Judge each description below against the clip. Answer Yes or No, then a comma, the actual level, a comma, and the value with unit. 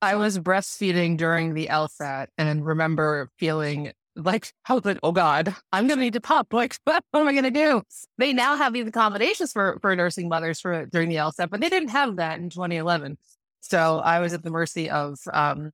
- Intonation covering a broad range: Yes, wide, 6.9 semitones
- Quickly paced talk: Yes, fast, 210 wpm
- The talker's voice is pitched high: No, medium, 175 Hz